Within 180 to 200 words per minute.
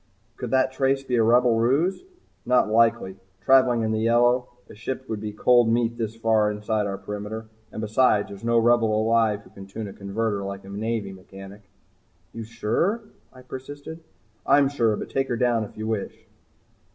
Yes: average, 185 wpm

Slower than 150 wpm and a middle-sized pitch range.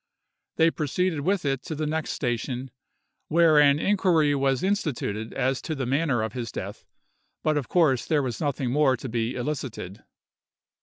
No: average, 165 wpm; average, 3.9 semitones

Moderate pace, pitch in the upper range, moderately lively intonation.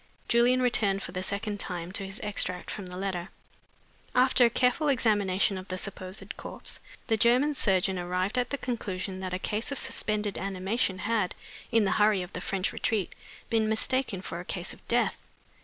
Yes: average, 185 wpm; high, 200 Hz; average, 3.7 semitones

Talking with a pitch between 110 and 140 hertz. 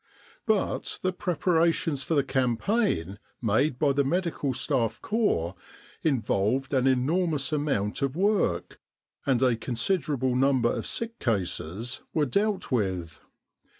Yes: low, 135 Hz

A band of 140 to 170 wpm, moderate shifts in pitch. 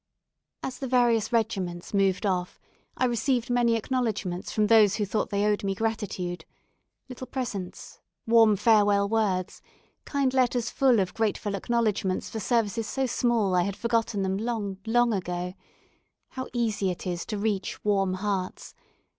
Yes: average, 155 wpm; average, 3.4 semitones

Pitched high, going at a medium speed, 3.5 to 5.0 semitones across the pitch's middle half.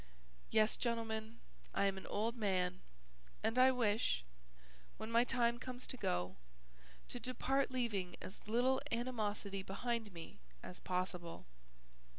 No: high, 220 Hz; slow, 130 wpm; average, 4.1 semitones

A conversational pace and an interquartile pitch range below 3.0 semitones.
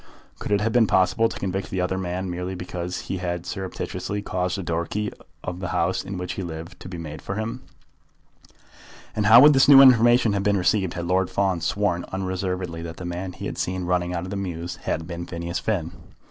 No: fast, 220 wpm; narrow, 2.4 semitones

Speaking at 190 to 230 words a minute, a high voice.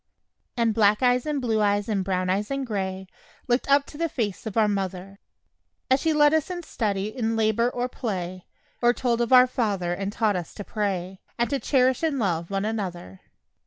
Yes: average, 200 wpm; high, 220 Hz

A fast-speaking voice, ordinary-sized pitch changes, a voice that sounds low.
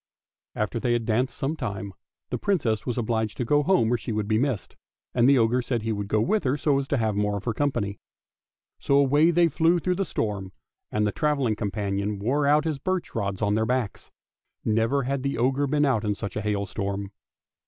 Yes: fast, 215 wpm; average, 5.0 semitones; low, 120 Hz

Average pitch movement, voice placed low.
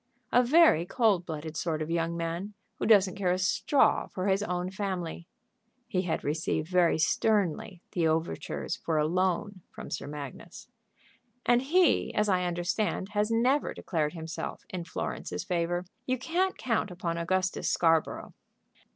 No: average, 3.9 semitones; medium, 180 Hz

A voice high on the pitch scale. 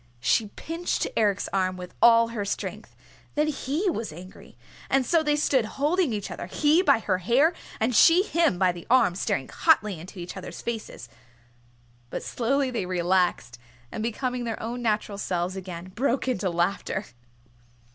Yes: high, 220 Hz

